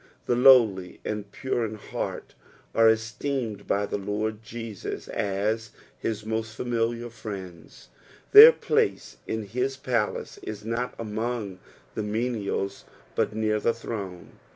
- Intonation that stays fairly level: Yes, narrow, 2.3 semitones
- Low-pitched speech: Yes, low, 110 Hz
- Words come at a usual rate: No, slow, 130 wpm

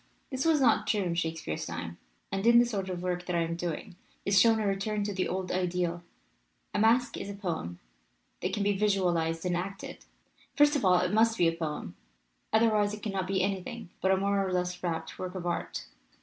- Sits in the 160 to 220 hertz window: Yes, high, 190 Hz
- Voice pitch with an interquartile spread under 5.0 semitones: Yes, average, 3.0 semitones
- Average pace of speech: No, fast, 215 wpm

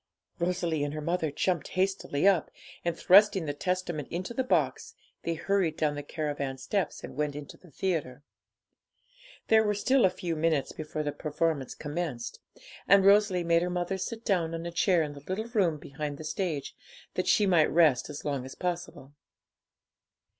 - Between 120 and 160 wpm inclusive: No, average, 175 wpm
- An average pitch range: Yes, average, 4.0 semitones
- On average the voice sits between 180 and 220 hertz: No, medium, 170 Hz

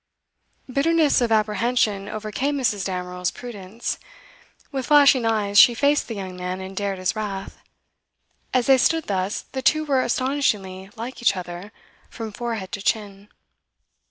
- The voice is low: No, high, 215 Hz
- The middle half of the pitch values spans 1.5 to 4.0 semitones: No, average, 4.9 semitones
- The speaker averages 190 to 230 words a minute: No, average, 145 wpm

